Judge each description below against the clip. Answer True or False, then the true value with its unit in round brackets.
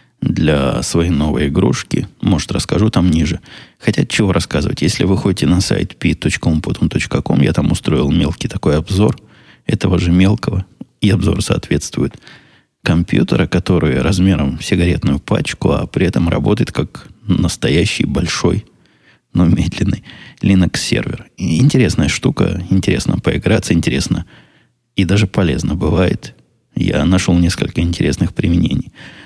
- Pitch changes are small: True (2.1 semitones)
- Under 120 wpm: False (125 wpm)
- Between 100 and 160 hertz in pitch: False (90 Hz)